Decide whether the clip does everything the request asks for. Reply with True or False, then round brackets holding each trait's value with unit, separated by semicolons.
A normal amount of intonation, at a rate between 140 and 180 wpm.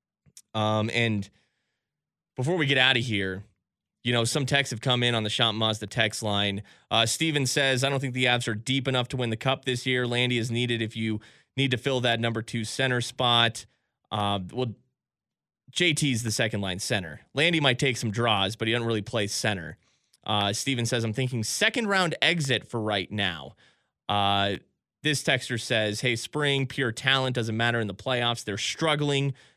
False (3.8 semitones; 195 wpm)